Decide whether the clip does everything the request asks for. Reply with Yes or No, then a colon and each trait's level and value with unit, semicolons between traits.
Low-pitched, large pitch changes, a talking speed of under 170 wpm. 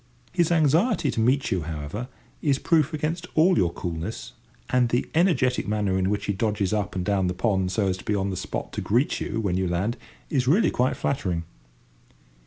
No: low, 110 Hz; wide, 7.0 semitones; average, 200 wpm